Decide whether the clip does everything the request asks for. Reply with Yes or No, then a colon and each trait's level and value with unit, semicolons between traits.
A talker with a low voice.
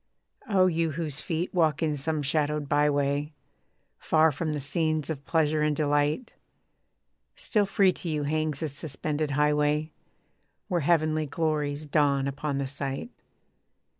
No: medium, 150 Hz